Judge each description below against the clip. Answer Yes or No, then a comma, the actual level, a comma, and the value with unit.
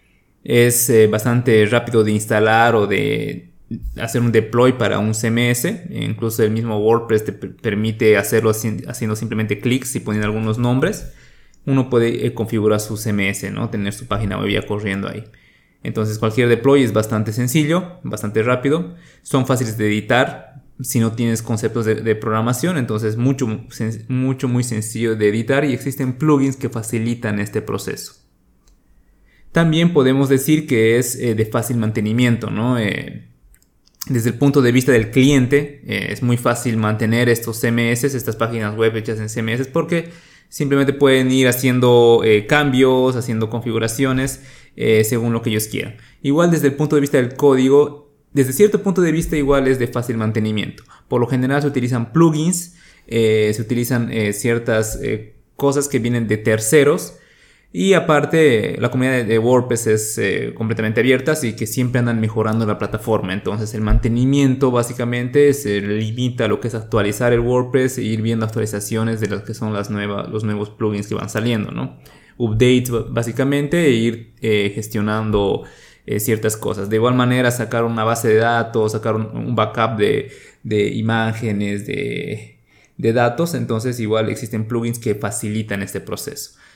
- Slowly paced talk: No, average, 155 wpm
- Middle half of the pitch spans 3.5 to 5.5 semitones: No, average, 3.1 semitones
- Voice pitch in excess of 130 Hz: No, low, 115 Hz